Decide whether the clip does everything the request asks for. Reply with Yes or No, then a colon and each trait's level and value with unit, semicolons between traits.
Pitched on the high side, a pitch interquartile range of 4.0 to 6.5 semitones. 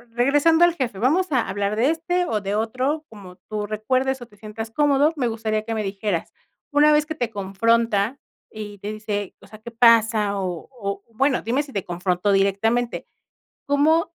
Yes: high, 225 Hz; average, 5.0 semitones